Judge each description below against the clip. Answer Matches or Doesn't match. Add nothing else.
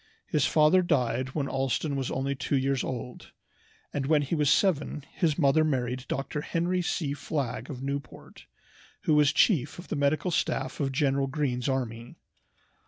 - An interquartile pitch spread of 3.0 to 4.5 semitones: Doesn't match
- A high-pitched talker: Doesn't match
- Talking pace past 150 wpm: Matches